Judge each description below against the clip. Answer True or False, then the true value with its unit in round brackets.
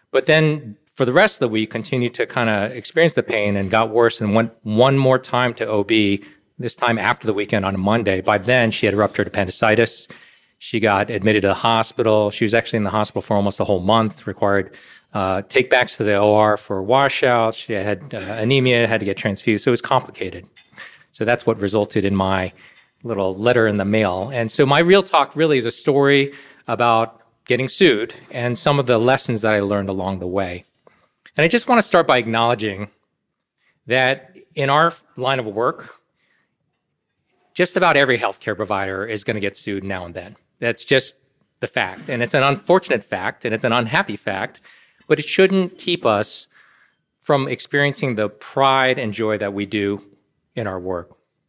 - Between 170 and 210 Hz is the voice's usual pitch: False (115 Hz)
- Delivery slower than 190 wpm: False (195 wpm)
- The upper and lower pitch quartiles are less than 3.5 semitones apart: False (4.4 semitones)